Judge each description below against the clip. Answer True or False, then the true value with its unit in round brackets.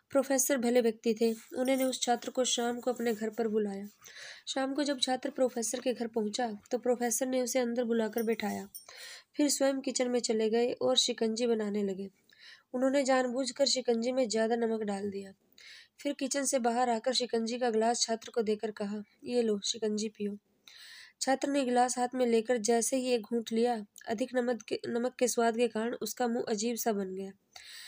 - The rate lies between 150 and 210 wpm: True (190 wpm)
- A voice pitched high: True (240 Hz)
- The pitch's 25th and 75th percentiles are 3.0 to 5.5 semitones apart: False (2.4 semitones)